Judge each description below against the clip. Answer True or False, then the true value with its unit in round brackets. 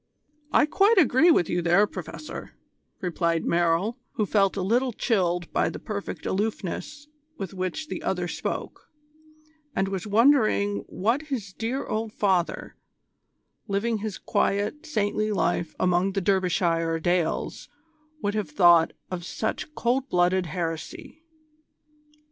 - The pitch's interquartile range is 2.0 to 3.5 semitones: False (4.3 semitones)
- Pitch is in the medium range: False (195 Hz)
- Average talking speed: False (130 wpm)